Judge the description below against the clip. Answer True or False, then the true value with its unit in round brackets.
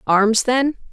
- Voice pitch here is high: True (230 Hz)